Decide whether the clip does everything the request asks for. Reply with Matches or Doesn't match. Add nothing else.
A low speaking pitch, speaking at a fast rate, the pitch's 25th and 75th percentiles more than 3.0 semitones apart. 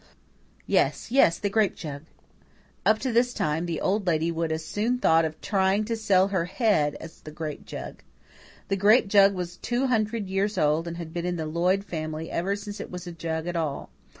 Doesn't match